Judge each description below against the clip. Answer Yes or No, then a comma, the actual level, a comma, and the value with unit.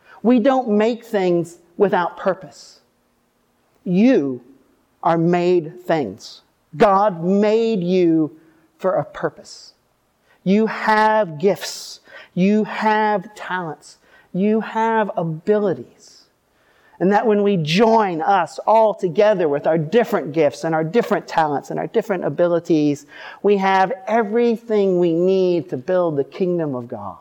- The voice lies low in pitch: No, high, 190 Hz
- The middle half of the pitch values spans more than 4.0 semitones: Yes, average, 4.4 semitones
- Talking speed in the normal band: No, slow, 125 wpm